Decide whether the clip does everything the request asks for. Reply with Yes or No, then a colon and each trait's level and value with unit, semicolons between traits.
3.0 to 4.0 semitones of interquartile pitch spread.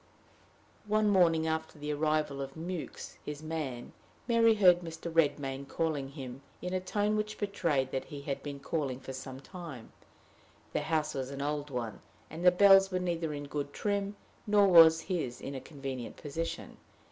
No: average, 4.5 semitones